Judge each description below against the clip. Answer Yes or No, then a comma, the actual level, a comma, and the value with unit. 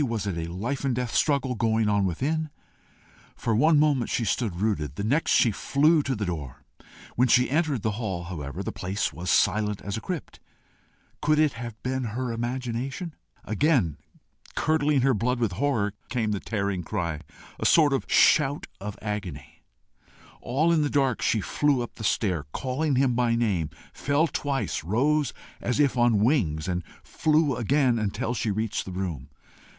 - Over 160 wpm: Yes, average, 175 wpm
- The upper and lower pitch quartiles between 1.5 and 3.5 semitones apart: No, wide, 5.6 semitones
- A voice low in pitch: Yes, low, 115 Hz